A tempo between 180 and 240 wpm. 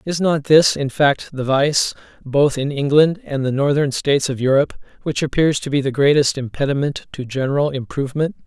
Yes: average, 185 wpm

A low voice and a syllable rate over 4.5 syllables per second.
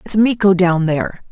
No: high, 190 Hz; 5.2 syllables/s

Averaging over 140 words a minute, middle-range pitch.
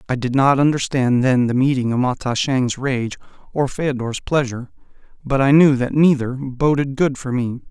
No: average, 180 wpm; low, 130 Hz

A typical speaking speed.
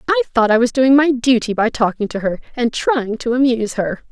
No: fast, 235 wpm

